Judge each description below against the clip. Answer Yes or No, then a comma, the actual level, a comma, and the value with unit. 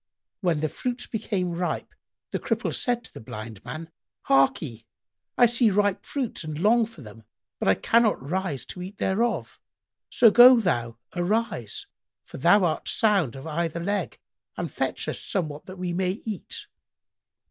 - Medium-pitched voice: Yes, medium, 180 Hz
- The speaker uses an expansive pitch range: Yes, wide, 6.5 semitones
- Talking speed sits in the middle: Yes, average, 160 wpm